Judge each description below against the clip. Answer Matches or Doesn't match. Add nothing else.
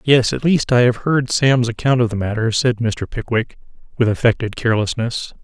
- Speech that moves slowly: Doesn't match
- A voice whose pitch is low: Matches